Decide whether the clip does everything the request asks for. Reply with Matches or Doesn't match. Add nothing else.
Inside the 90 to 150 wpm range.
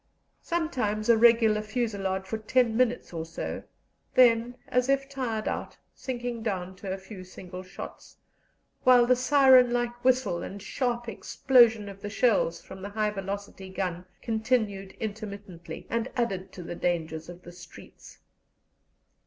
Matches